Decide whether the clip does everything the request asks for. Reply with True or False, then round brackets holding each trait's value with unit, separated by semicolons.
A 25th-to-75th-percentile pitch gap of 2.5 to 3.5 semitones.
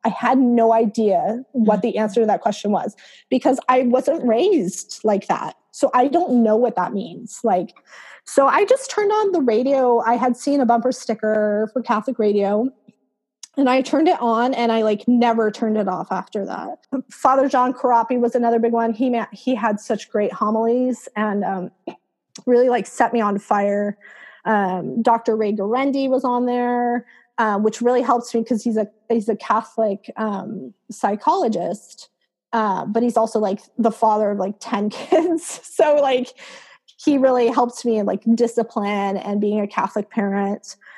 True (2.9 semitones)